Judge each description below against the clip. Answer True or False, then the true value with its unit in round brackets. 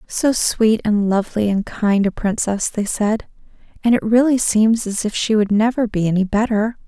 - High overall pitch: True (215 Hz)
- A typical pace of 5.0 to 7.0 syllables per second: False (4.8 syllables/s)